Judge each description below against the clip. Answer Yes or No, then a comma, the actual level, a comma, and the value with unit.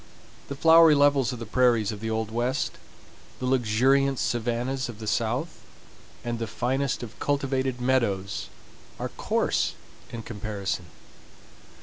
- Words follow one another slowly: Yes, slow, 130 wpm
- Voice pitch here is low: Yes, low, 120 Hz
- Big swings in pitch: No, average, 3.2 semitones